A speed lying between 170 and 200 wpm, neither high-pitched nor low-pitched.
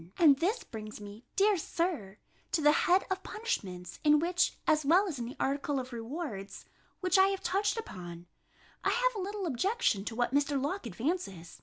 No: average, 185 wpm; very high, 295 Hz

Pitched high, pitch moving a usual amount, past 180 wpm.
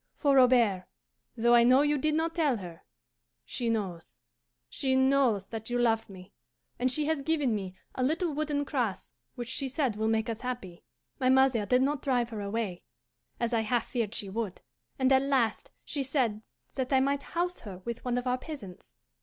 Yes: high, 245 Hz; average, 3.9 semitones; average, 195 wpm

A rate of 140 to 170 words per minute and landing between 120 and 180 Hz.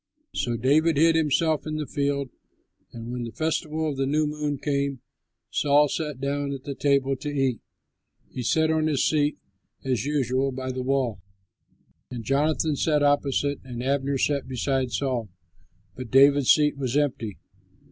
Yes: average, 160 wpm; medium, 140 Hz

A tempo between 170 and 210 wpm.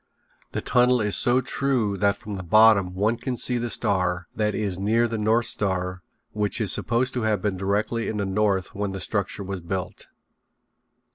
Yes: average, 190 wpm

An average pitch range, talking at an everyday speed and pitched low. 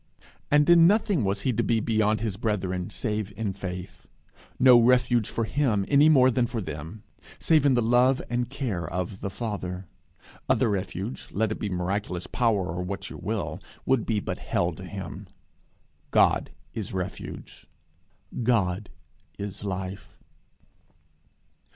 Yes: average, 4.4 semitones; average, 150 wpm; low, 110 Hz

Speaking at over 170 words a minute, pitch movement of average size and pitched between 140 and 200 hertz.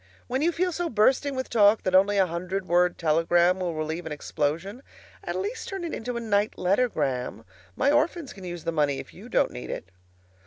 No: fast, 205 wpm; wide, 7.2 semitones; high, 190 Hz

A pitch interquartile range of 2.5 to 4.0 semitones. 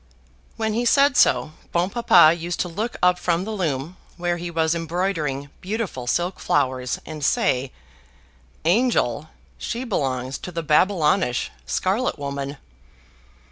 No: average, 5.3 semitones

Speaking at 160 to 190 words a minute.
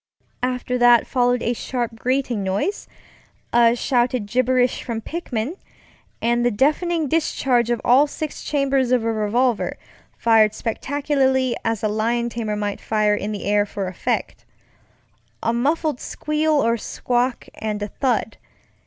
No: average, 140 wpm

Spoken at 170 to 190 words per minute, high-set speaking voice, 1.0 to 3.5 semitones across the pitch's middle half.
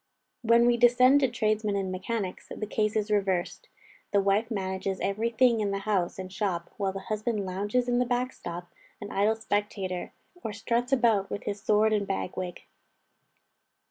Yes: average, 175 wpm; high, 210 Hz; average, 3.1 semitones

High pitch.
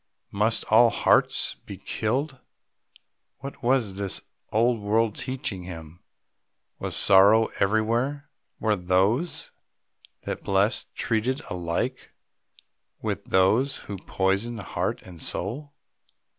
No: low, 110 Hz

